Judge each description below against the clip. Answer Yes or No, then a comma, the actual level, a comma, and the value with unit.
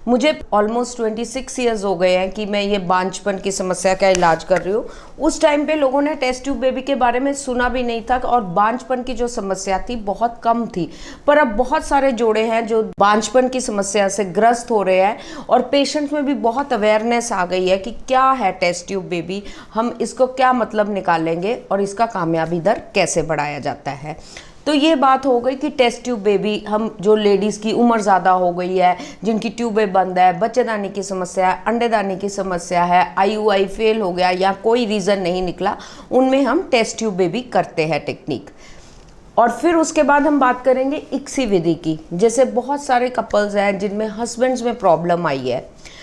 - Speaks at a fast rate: Yes, fast, 210 wpm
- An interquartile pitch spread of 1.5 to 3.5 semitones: No, average, 4.9 semitones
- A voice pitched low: No, high, 220 Hz